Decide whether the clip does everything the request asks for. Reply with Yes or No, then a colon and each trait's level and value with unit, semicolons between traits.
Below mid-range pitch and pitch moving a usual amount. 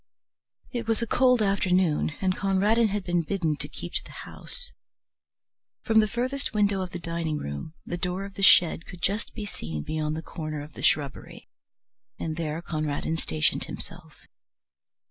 No: medium, 175 Hz; average, 4.7 semitones